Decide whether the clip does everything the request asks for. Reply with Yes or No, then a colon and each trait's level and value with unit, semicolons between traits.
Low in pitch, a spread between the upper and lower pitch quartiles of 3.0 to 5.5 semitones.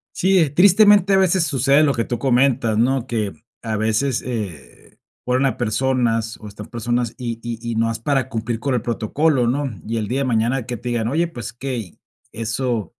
Yes: low, 120 Hz; average, 3.3 semitones